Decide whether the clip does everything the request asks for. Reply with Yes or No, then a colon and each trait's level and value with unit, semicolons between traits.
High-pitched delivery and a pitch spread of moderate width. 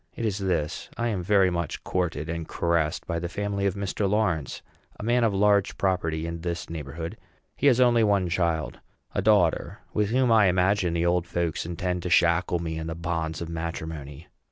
No: very low, 85 Hz; average, 3.3 semitones